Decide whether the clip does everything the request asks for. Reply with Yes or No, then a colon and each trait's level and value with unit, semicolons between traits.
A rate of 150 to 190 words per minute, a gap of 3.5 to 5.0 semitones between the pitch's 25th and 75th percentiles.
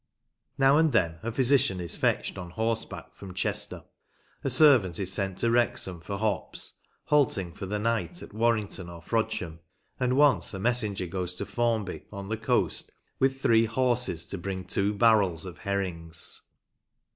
Yes: average, 160 wpm; average, 4.2 semitones